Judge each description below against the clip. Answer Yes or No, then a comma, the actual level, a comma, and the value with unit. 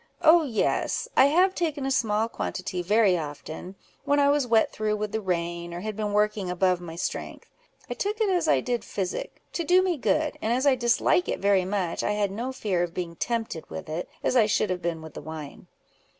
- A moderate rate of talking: No, fast, 220 wpm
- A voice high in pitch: Yes, high, 210 Hz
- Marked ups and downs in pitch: Yes, wide, 6.9 semitones